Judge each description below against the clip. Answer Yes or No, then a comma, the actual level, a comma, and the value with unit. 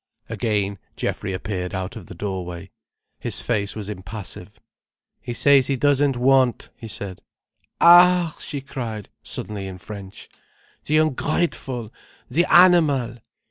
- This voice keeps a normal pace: No, slow, 125 wpm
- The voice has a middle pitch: No, low, 115 Hz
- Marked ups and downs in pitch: Yes, wide, 6.2 semitones